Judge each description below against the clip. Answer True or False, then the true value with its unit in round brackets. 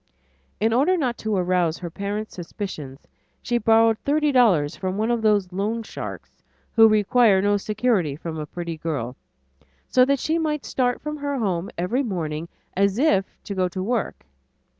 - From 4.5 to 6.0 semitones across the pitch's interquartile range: True (5.3 semitones)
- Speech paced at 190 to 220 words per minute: False (165 wpm)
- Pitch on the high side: True (205 Hz)